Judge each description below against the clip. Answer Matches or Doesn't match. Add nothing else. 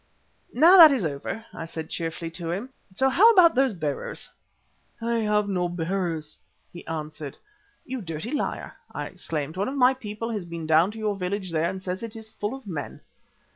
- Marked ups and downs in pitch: Matches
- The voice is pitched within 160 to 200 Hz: Matches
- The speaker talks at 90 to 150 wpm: Doesn't match